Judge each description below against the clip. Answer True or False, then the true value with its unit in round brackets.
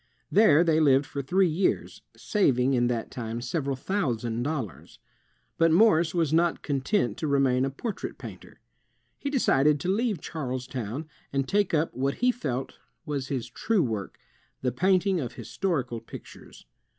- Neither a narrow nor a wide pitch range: False (5.7 semitones)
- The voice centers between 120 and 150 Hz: True (140 Hz)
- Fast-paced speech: False (150 wpm)